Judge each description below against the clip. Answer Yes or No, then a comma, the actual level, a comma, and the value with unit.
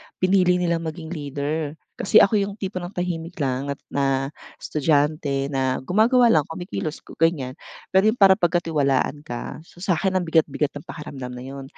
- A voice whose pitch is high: No, medium, 160 Hz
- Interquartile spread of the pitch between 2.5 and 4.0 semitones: No, average, 4.4 semitones